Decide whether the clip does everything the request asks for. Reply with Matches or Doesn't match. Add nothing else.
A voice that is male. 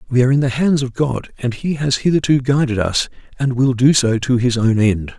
Matches